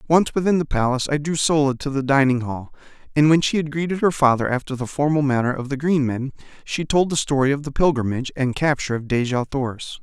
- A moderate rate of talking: No, fast, 225 wpm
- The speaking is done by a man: Yes, male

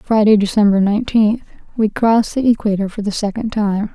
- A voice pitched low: No, high, 215 Hz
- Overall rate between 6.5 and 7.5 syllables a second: No, 5.5 syllables/s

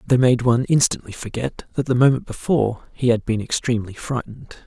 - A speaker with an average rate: Yes, average, 180 wpm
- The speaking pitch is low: Yes, low, 120 Hz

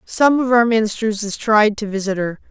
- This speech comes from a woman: Yes, female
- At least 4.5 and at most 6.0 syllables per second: Yes, 5.2 syllables/s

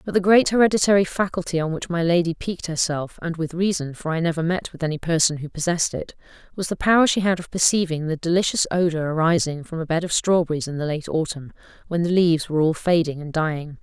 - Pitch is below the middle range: No, medium, 170 Hz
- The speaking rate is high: Yes, fast, 225 wpm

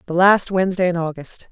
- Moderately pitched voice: Yes, medium, 180 Hz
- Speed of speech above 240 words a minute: No, average, 200 wpm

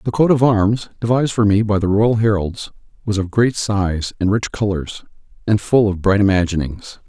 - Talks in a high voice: No, low, 105 Hz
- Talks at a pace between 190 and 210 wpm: Yes, average, 195 wpm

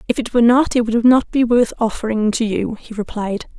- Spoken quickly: Yes, fast, 235 wpm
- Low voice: No, high, 230 Hz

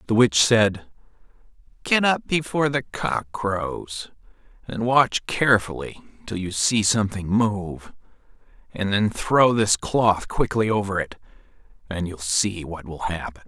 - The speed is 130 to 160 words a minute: Yes, average, 140 wpm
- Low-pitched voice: Yes, low, 105 Hz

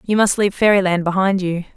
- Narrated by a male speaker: No, female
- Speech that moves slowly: No, fast, 205 wpm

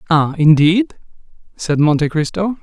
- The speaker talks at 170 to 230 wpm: No, slow, 115 wpm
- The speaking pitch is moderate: Yes, medium, 165 Hz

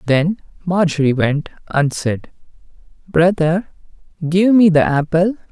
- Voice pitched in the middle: Yes, medium, 165 Hz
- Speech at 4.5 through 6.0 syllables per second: No, 3.9 syllables/s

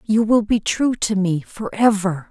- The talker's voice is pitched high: Yes, high, 205 Hz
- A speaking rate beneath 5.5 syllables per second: Yes, 4.1 syllables/s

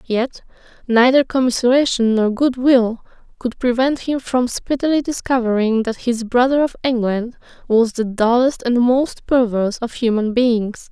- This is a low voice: No, high, 240 Hz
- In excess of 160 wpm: No, average, 145 wpm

